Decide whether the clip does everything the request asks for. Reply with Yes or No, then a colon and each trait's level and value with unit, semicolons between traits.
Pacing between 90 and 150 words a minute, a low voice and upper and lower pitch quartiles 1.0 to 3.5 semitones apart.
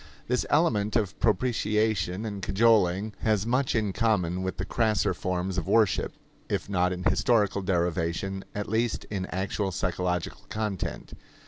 Yes: average, 140 wpm; low, 100 Hz; average, 3.0 semitones